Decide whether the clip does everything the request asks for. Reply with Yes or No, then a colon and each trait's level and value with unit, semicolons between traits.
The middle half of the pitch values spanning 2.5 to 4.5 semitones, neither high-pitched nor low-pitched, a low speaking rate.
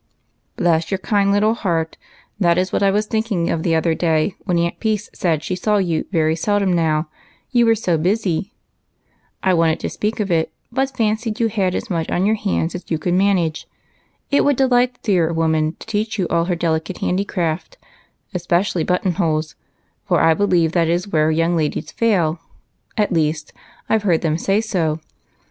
No: average, 4.2 semitones; medium, 180 Hz; average, 190 wpm